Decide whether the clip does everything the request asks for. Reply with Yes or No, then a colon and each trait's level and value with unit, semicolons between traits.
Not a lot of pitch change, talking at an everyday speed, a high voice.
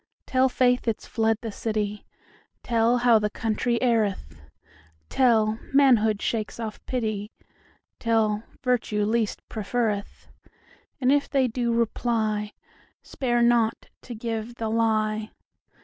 No: narrow, 2.0 semitones; slow, 100 wpm; high, 225 Hz